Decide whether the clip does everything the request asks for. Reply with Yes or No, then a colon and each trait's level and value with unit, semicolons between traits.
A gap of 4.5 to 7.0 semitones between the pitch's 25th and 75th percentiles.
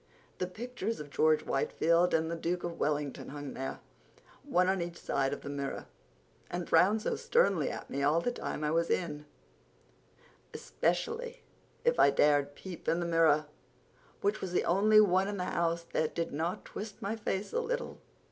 Yes: average, 5.1 semitones